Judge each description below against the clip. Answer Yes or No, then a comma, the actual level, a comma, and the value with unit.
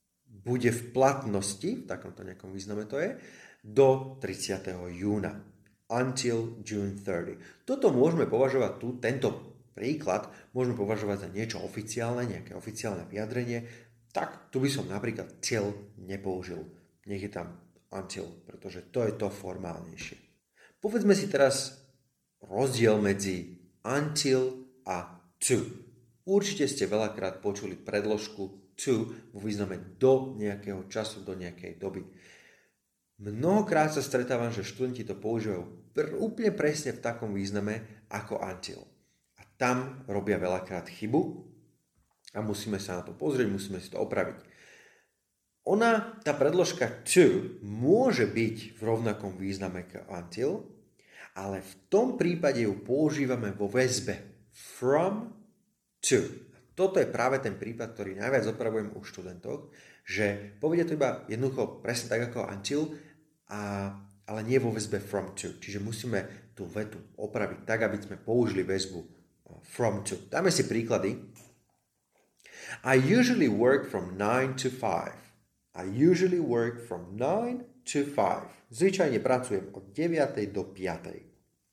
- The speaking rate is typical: Yes, average, 130 wpm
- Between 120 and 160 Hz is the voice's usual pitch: No, low, 110 Hz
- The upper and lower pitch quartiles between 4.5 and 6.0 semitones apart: Yes, average, 4.9 semitones